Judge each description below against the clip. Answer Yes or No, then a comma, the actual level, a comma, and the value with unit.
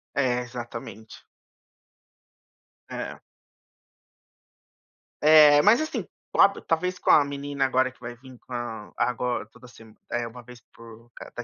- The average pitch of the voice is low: Yes, low, 125 Hz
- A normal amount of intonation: Yes, average, 3.0 semitones